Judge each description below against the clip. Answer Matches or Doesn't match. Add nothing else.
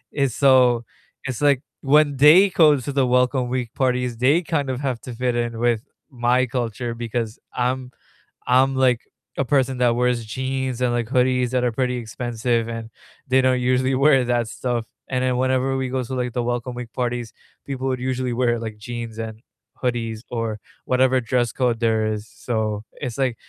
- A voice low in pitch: Matches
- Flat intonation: Matches